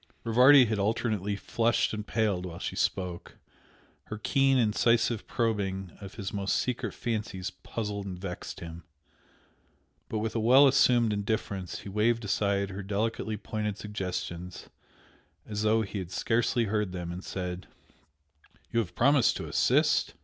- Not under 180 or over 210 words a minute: No, average, 145 wpm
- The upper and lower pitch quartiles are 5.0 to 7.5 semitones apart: No, average, 3.0 semitones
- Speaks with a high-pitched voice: No, low, 105 Hz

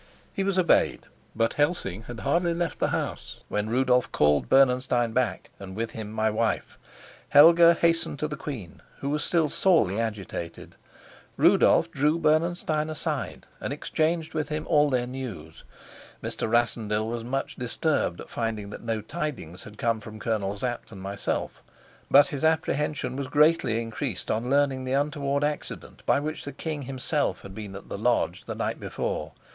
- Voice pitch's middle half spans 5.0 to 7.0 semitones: Yes, wide, 5.6 semitones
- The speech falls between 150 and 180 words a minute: Yes, average, 165 wpm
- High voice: No, low, 130 Hz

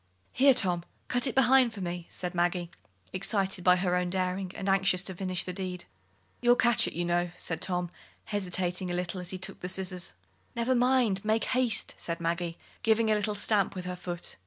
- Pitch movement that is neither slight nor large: Yes, average, 3.2 semitones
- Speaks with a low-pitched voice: No, medium, 185 Hz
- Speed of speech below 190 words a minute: No, average, 200 wpm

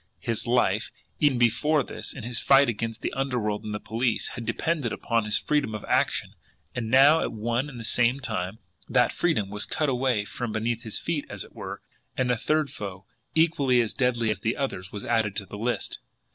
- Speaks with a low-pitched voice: Yes, low, 120 Hz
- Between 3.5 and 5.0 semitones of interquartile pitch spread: Yes, average, 3.9 semitones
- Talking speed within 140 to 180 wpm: No, fast, 205 wpm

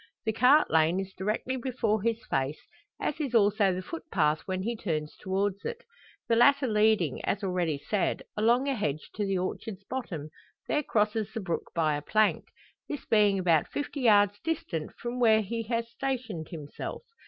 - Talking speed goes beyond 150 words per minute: Yes, average, 175 wpm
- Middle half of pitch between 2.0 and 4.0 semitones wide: No, average, 4.4 semitones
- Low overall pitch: No, high, 210 Hz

